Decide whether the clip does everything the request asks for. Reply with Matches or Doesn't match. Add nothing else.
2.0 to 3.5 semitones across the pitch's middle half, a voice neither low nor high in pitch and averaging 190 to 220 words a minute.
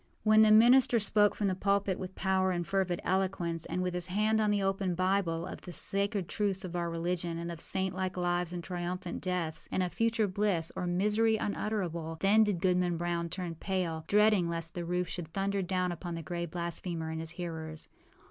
Matches